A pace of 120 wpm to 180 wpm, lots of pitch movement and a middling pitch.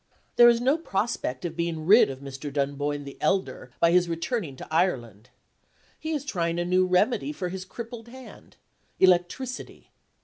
Yes: average, 165 wpm; wide, 8.2 semitones; medium, 180 Hz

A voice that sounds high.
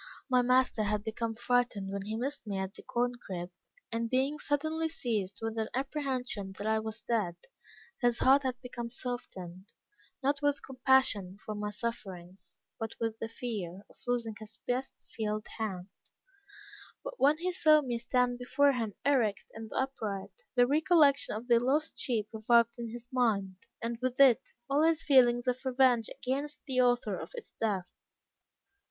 Yes: high, 240 Hz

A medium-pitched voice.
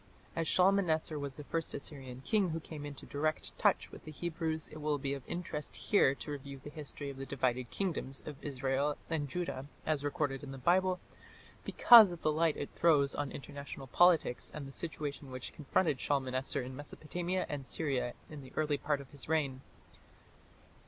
Yes: medium, 145 Hz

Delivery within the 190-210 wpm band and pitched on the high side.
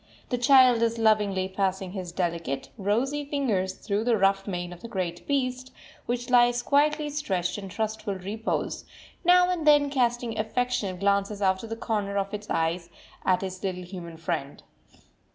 No: average, 165 wpm; high, 205 Hz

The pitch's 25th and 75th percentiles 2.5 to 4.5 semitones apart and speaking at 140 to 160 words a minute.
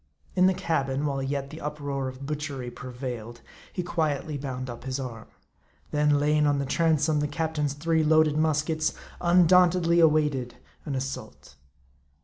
Yes: average, 2.8 semitones; average, 145 wpm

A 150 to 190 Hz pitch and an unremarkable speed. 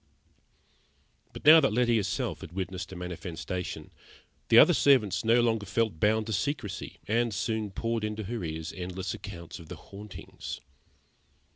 No: low, 105 Hz; average, 150 wpm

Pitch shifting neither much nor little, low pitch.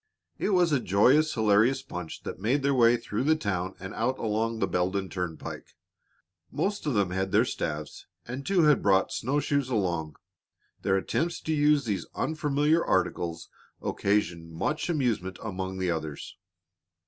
No: wide, 7.4 semitones; low, 110 Hz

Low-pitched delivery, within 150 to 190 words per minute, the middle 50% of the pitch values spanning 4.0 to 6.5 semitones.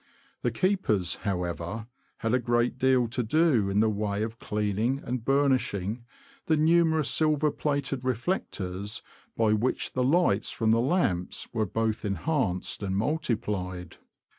No: low, 115 Hz; average, 140 wpm; average, 5.1 semitones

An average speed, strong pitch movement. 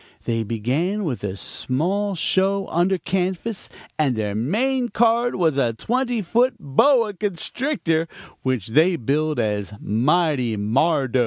No: slow, 130 wpm; wide, 8.8 semitones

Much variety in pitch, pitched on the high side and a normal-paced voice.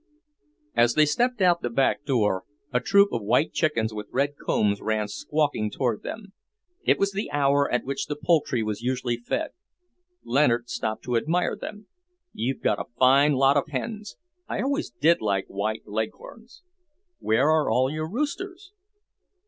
No: wide, 6.7 semitones; medium, 140 Hz; average, 165 wpm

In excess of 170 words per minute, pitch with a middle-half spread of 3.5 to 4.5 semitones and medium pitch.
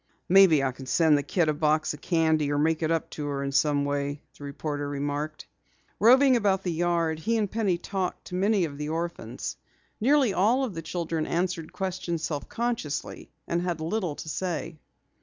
Yes: average, 195 wpm; average, 4.1 semitones; medium, 165 Hz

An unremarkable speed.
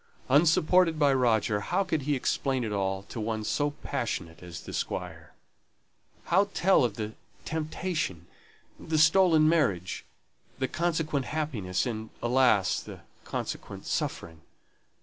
No: slow, 130 wpm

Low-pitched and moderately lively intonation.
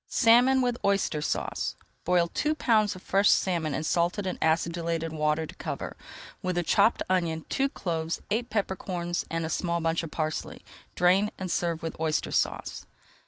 No: medium, 175 Hz; average, 3.5 semitones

